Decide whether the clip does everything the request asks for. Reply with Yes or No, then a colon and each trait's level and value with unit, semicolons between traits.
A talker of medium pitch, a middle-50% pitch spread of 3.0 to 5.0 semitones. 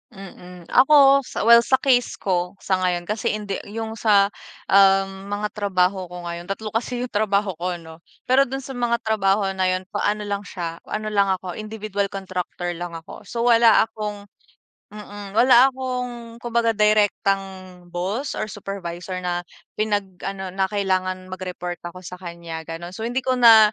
No: high, 200 Hz; average, 3.5 semitones